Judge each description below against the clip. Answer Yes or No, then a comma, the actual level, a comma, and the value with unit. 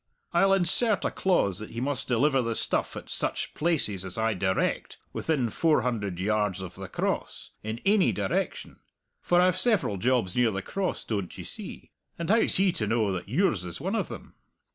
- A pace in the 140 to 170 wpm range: No, average, 190 wpm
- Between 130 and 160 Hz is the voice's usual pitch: No, low, 115 Hz